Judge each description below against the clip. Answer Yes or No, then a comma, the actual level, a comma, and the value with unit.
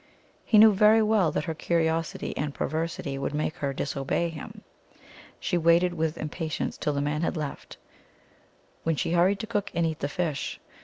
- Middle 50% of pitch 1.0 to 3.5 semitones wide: Yes, average, 2.9 semitones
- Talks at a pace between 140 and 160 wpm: No, average, 185 wpm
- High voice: No, medium, 165 Hz